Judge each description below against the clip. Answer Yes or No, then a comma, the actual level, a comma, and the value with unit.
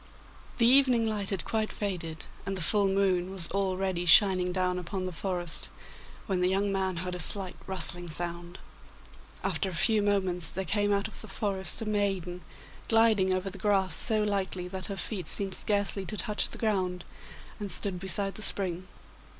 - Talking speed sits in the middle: Yes, average, 180 wpm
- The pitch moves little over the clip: Yes, narrow, 2.1 semitones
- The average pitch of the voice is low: No, high, 190 Hz